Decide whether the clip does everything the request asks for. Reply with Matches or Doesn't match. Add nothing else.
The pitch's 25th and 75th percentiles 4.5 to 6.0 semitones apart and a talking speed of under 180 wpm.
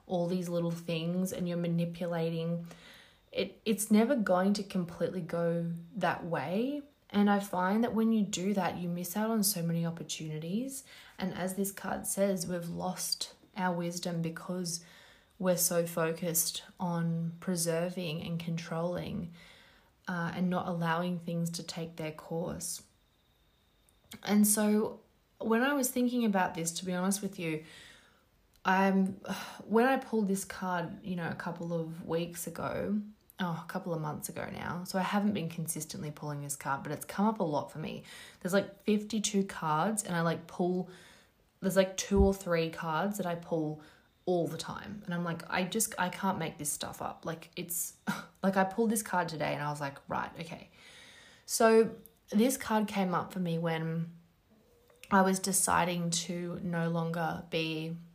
Doesn't match